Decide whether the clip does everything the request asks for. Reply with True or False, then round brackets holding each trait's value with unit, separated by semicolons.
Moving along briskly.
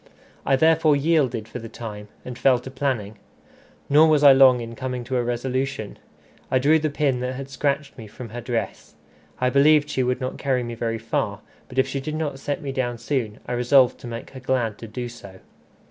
True (215 wpm)